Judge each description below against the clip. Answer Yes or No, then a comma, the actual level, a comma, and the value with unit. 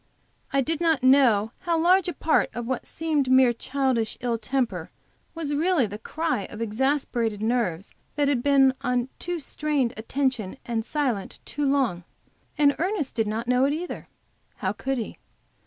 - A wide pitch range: No, average, 4.2 semitones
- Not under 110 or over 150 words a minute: No, average, 170 wpm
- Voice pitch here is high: Yes, very high, 265 Hz